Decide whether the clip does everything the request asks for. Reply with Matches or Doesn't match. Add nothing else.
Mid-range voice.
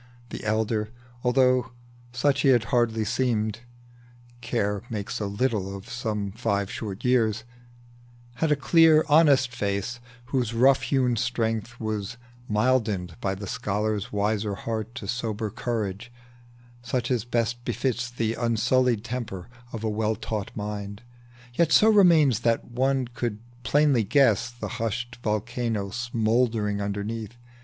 Doesn't match